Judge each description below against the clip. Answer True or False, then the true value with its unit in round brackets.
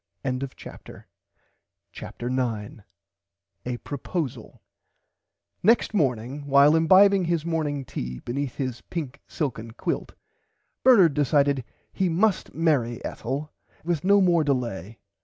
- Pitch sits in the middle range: True (145 Hz)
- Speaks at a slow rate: True (110 wpm)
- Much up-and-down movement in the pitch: False (5.0 semitones)